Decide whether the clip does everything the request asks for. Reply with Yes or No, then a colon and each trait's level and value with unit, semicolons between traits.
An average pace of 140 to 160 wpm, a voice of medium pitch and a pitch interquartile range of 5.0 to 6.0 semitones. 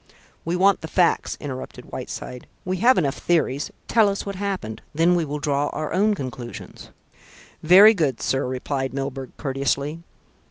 Yes: average, 155 wpm; medium, 150 Hz; wide, 5.4 semitones